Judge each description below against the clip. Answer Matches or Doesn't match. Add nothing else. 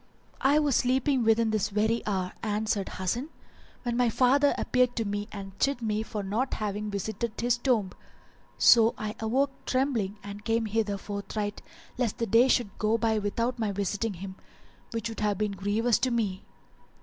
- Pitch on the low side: Doesn't match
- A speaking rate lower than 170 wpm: Doesn't match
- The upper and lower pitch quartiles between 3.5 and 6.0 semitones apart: Doesn't match